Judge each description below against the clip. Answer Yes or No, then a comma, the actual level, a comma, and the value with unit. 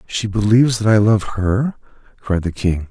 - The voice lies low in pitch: Yes, low, 105 Hz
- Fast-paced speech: No, average, 185 wpm